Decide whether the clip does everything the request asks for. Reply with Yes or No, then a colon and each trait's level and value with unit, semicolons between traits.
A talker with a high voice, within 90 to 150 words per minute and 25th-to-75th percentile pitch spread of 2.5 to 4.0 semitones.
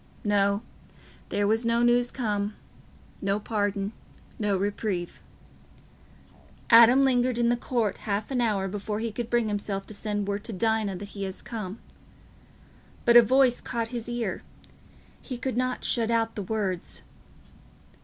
Yes: high, 220 Hz; average, 145 wpm; average, 2.9 semitones